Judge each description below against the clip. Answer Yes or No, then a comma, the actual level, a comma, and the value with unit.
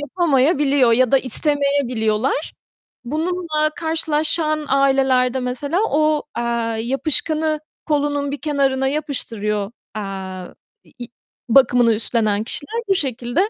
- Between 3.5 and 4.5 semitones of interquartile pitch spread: Yes, average, 4.0 semitones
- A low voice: No, very high, 275 Hz